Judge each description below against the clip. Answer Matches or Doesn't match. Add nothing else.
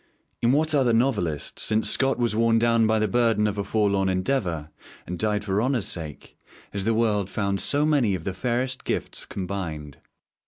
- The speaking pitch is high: Doesn't match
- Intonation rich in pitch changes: Doesn't match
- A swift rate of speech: Doesn't match